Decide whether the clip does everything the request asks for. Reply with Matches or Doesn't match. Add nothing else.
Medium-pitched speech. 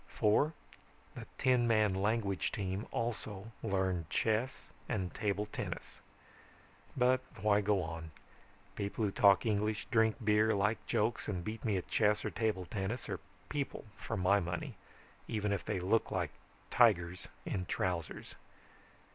Doesn't match